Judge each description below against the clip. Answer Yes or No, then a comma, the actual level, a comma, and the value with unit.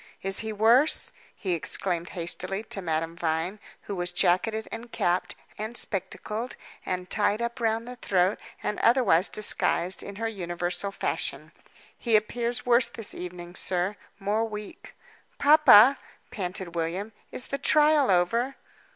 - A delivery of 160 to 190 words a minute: No, average, 140 wpm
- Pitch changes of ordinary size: Yes, average, 4.5 semitones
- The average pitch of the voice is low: No, high, 205 Hz